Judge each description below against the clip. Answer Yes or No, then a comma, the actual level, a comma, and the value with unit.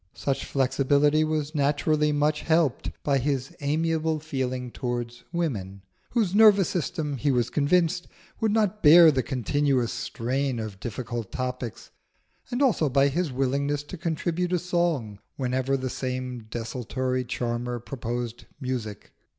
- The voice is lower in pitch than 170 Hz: Yes, medium, 140 Hz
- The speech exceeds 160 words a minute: No, slow, 135 wpm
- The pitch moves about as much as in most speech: Yes, average, 4.0 semitones